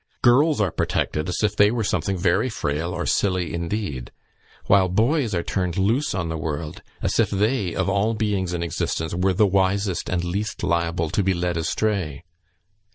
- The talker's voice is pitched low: Yes, very low, 95 Hz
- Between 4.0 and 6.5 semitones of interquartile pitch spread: No, average, 3.6 semitones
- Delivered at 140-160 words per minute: No, average, 180 wpm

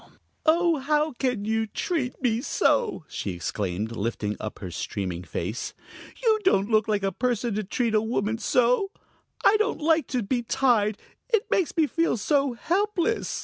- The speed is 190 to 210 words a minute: No, average, 165 wpm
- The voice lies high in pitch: Yes, high, 240 Hz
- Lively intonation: Yes, wide, 7.9 semitones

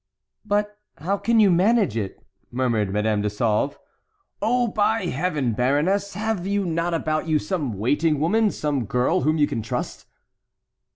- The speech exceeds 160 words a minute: No, average, 155 wpm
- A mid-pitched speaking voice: Yes, medium, 160 Hz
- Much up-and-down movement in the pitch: Yes, wide, 8.4 semitones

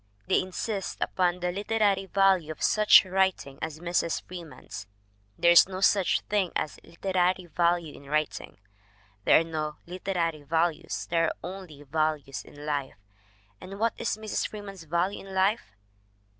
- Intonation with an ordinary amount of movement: Yes, average, 3.6 semitones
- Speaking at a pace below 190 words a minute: Yes, average, 150 wpm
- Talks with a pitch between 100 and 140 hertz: No, medium, 175 Hz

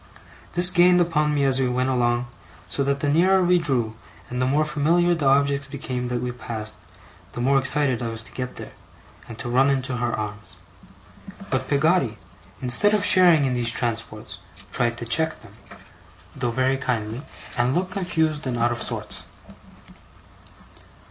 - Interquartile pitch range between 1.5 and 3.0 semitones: No, average, 4.3 semitones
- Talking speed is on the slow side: No, average, 170 wpm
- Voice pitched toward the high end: No, low, 135 Hz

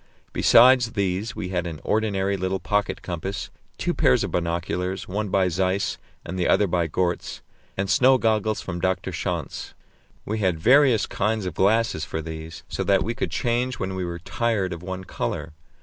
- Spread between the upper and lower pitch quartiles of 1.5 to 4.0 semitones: Yes, average, 3.5 semitones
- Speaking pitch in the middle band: No, very low, 95 Hz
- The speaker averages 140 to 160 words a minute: No, average, 180 wpm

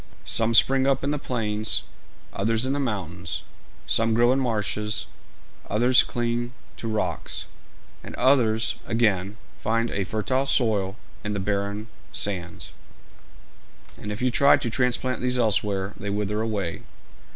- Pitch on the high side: No, low, 110 Hz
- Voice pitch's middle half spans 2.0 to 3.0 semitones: No, average, 3.4 semitones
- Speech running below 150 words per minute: Yes, average, 140 wpm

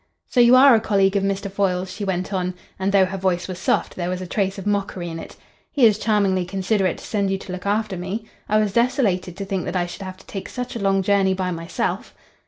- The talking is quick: Yes, fast, 255 wpm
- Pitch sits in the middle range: No, high, 195 Hz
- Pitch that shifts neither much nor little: No, narrow, 2.0 semitones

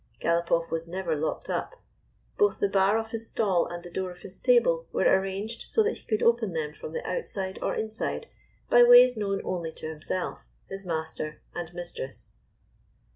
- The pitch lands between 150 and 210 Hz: Yes, high, 190 Hz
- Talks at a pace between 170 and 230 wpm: Yes, average, 180 wpm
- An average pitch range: Yes, average, 5.0 semitones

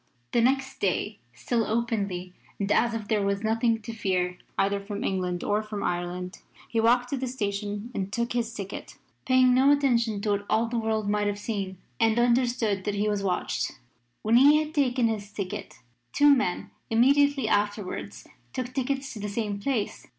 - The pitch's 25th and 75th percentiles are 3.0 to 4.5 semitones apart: Yes, average, 3.4 semitones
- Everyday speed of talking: Yes, average, 180 wpm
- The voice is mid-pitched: No, high, 220 Hz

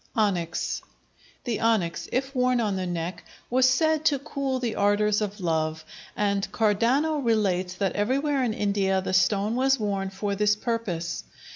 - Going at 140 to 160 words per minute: Yes, average, 155 wpm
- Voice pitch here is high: Yes, high, 210 Hz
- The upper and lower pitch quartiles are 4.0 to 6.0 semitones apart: Yes, average, 4.8 semitones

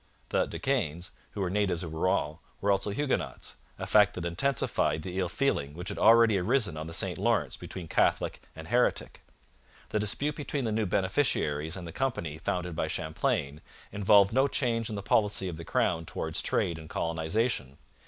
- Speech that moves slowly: No, average, 185 wpm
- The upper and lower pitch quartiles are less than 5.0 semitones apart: No, wide, 5.5 semitones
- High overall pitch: No, very low, 95 Hz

